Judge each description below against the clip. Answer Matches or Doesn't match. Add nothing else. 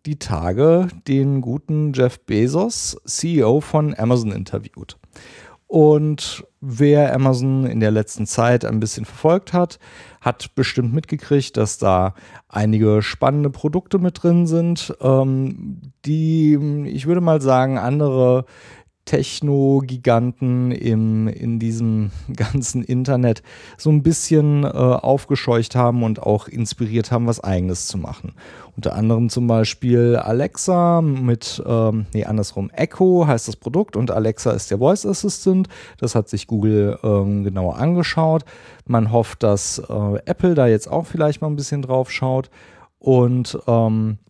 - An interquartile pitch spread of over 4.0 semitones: Matches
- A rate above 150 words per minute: Doesn't match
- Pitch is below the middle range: Matches